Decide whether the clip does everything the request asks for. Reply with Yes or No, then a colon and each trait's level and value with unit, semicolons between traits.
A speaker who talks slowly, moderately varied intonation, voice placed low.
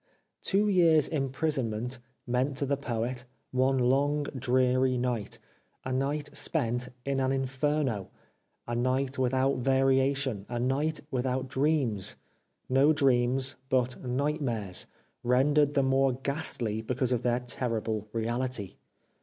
No: slow, 125 wpm; narrow, 2.2 semitones; low, 130 Hz